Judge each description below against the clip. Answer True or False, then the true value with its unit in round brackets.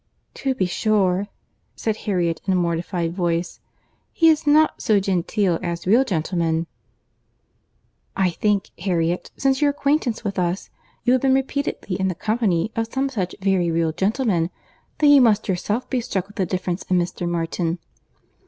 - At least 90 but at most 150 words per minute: False (160 wpm)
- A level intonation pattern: False (5.0 semitones)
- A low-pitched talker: False (190 Hz)